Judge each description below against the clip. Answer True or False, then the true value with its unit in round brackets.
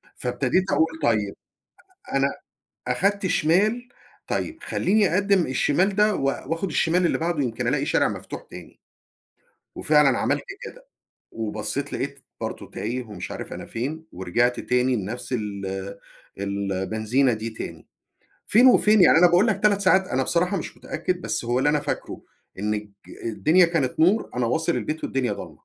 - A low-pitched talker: False (145 Hz)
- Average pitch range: False (8.1 semitones)